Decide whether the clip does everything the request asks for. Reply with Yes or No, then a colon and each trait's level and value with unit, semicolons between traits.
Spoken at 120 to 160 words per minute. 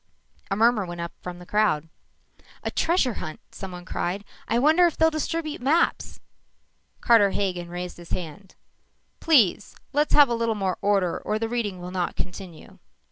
No: average, 170 wpm